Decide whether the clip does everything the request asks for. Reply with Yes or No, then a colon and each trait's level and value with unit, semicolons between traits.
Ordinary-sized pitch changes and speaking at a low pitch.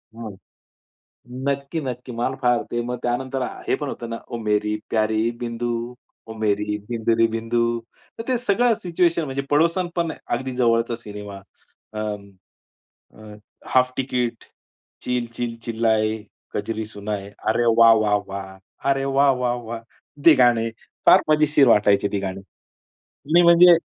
Yes: average, 4.1 semitones; low, 120 Hz